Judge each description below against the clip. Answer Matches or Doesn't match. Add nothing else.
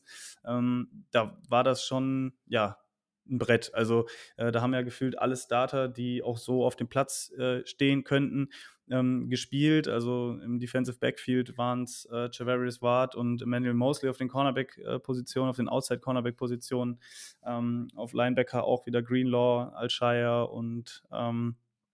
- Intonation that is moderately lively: Doesn't match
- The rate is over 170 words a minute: Doesn't match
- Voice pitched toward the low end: Matches